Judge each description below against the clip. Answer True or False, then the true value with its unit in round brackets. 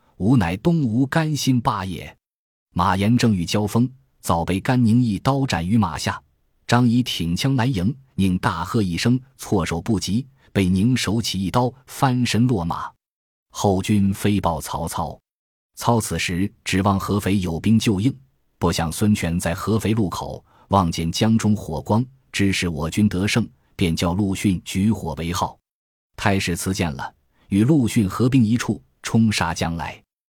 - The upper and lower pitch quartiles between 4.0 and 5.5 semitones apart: True (5.1 semitones)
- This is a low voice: True (105 Hz)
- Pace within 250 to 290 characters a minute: False (220 characters per minute)